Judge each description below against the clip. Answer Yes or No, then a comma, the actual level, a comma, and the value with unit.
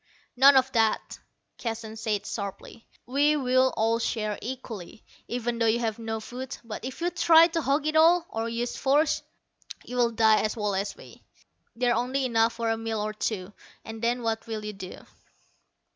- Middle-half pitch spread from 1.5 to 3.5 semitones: Yes, average, 2.9 semitones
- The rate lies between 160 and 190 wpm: Yes, average, 175 wpm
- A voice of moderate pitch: No, high, 230 Hz